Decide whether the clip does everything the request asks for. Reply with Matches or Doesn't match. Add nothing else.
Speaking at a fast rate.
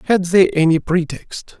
Doesn't match